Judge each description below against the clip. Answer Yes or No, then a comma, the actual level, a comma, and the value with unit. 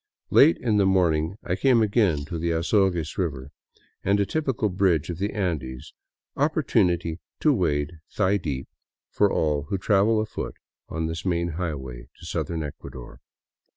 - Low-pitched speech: Yes, very low, 85 Hz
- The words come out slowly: No, average, 155 wpm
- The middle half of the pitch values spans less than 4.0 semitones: No, average, 4.6 semitones